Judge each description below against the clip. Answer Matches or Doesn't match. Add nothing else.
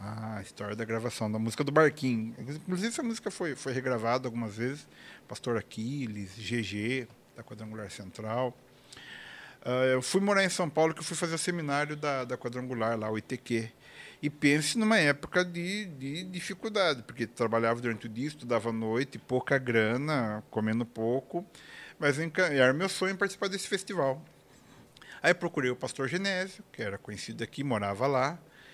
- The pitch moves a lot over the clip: Matches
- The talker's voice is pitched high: Doesn't match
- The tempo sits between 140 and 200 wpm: Matches